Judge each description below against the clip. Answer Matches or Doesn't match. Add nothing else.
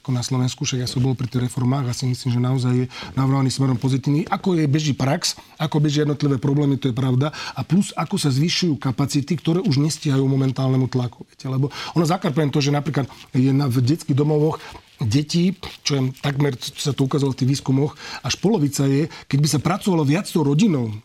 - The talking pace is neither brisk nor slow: Doesn't match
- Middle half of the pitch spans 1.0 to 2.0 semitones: Doesn't match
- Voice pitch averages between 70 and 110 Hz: Doesn't match